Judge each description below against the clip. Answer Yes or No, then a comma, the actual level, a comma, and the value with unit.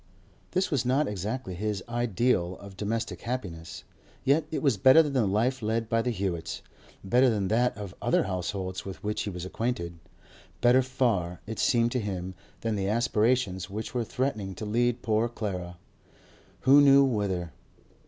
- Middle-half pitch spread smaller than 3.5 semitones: No, average, 4.7 semitones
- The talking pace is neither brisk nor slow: Yes, average, 155 wpm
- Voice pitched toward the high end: No, low, 110 Hz